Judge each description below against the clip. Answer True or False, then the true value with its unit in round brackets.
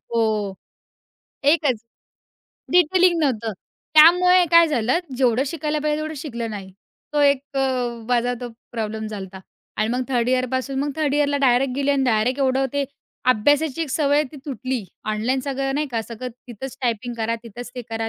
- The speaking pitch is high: True (260 Hz)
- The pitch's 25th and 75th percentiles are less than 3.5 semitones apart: False (4.0 semitones)